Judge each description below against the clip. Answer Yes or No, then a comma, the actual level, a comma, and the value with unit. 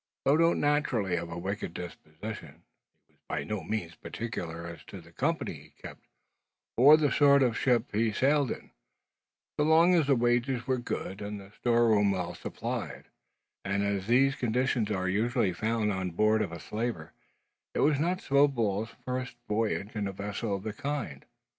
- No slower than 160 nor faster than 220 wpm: Yes, average, 180 wpm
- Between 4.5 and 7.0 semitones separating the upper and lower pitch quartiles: Yes, average, 4.8 semitones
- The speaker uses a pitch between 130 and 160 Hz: No, low, 110 Hz